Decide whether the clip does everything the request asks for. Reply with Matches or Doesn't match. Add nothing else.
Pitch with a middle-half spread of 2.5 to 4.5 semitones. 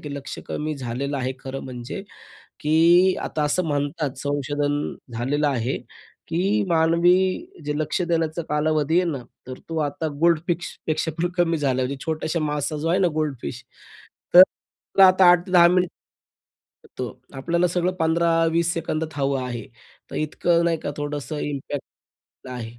Matches